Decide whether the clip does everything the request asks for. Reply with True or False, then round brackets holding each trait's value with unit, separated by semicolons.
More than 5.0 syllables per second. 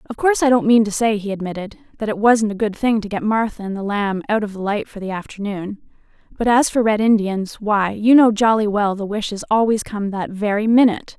True (5.7 syllables/s)